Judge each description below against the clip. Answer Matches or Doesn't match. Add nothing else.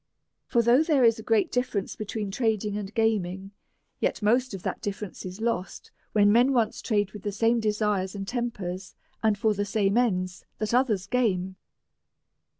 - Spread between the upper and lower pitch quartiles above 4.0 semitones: Doesn't match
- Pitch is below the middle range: Doesn't match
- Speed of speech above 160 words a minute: Matches